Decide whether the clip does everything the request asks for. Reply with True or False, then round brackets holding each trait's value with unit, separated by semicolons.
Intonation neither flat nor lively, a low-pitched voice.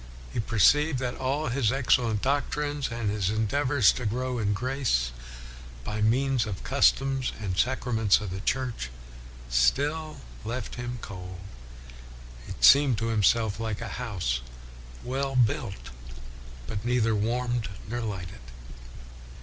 True (4.0 semitones; 115 Hz)